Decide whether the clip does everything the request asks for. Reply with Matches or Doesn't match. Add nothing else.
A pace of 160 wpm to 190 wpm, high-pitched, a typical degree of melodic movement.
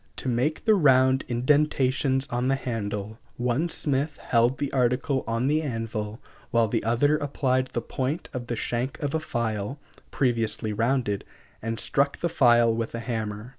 Doesn't match